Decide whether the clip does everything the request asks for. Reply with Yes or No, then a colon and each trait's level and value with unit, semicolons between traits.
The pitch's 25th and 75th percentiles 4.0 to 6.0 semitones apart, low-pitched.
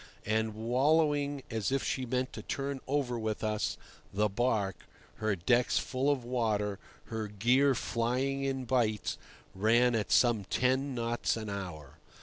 No: average, 3.5 semitones; low, 120 Hz